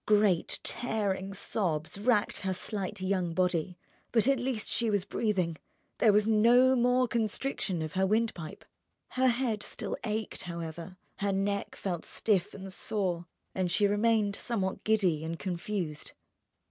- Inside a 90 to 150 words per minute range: Yes, average, 140 wpm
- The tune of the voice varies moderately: Yes, average, 3.4 semitones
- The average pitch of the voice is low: No, high, 200 Hz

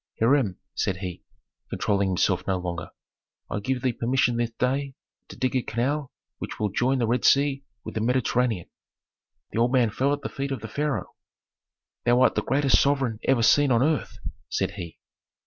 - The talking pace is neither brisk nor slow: Yes, average, 180 wpm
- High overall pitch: No, low, 125 Hz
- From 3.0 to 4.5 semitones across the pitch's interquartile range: Yes, average, 3.6 semitones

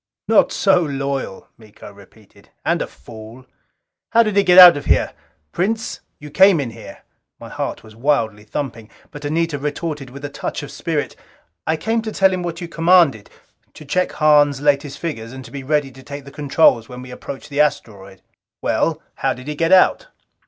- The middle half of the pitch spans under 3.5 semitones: No, average, 4.9 semitones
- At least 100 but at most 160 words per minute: No, average, 190 wpm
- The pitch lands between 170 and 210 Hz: No, medium, 145 Hz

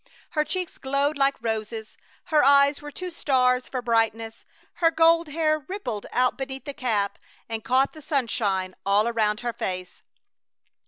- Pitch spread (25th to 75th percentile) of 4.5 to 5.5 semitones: Yes, average, 4.8 semitones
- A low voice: No, very high, 255 Hz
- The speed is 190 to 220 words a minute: No, average, 155 wpm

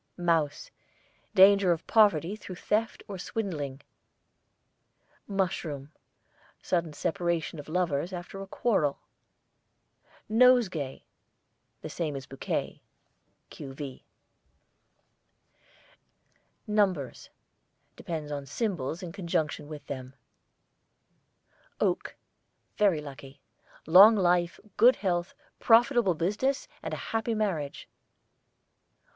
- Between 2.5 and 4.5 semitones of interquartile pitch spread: No, wide, 5.5 semitones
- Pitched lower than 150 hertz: No, medium, 175 Hz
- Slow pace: Yes, slow, 90 wpm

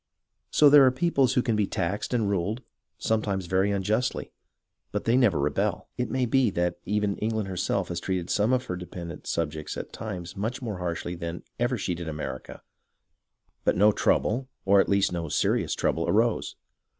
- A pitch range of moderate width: Yes, average, 4.8 semitones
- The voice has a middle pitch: No, low, 100 Hz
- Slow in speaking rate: No, average, 180 wpm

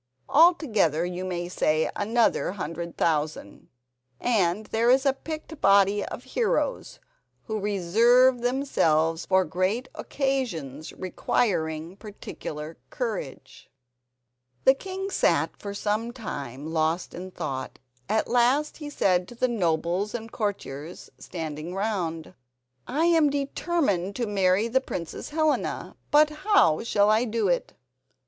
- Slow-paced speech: Yes, slow, 125 wpm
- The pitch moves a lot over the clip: Yes, wide, 6.9 semitones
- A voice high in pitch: Yes, high, 205 Hz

